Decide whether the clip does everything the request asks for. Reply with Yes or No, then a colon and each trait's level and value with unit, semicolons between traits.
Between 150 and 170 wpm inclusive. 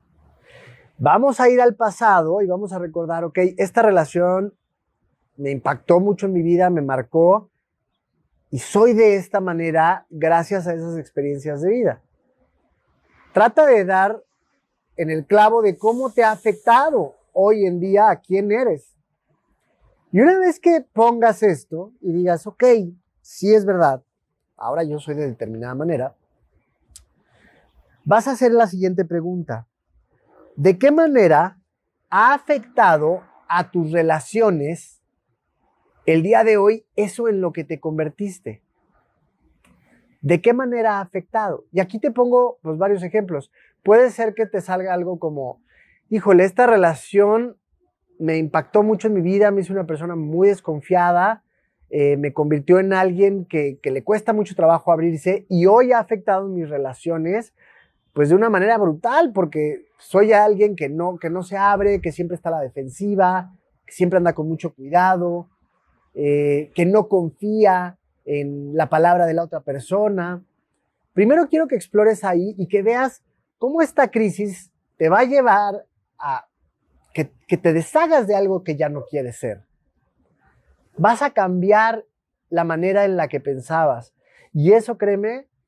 Yes: average, 155 wpm